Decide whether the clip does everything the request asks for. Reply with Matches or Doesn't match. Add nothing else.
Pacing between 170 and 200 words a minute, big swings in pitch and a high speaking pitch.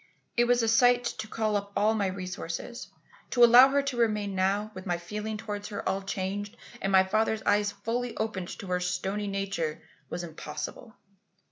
Doesn't match